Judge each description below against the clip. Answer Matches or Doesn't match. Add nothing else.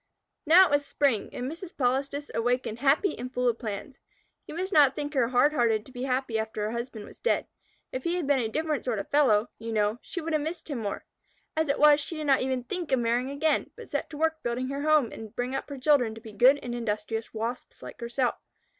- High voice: Matches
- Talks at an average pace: Doesn't match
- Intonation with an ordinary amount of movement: Matches